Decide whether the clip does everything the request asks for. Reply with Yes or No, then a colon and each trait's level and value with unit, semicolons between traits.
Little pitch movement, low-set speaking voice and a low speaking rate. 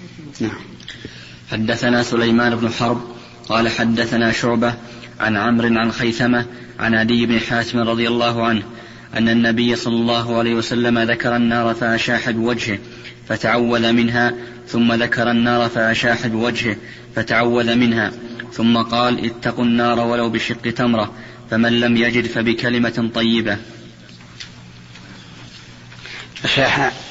No: narrow, 0.8 semitones; low, 115 Hz; average, 110 wpm